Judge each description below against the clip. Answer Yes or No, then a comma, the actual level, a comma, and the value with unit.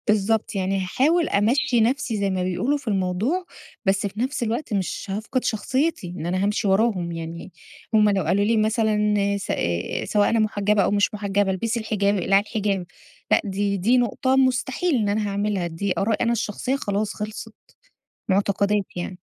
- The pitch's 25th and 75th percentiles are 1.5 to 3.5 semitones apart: Yes, average, 3.0 semitones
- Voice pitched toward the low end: No, high, 205 Hz